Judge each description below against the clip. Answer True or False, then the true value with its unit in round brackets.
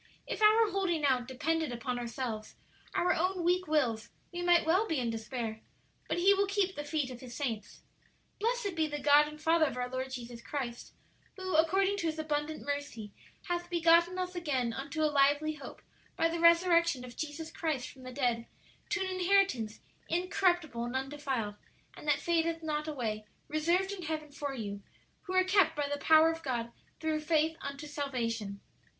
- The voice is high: True (305 Hz)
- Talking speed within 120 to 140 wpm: False (180 wpm)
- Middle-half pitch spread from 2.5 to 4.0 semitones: False (5.2 semitones)